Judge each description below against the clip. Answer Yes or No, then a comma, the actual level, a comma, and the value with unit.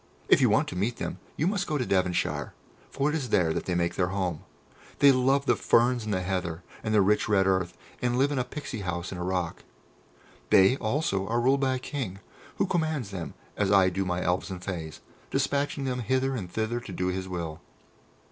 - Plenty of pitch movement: Yes, wide, 6.2 semitones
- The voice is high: No, low, 105 Hz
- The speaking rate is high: Yes, fast, 220 wpm